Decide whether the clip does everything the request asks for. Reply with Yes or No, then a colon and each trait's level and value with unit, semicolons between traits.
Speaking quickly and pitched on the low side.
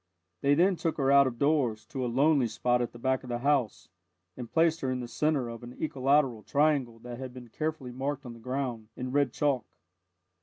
Yes: fast, 220 wpm; low, 130 Hz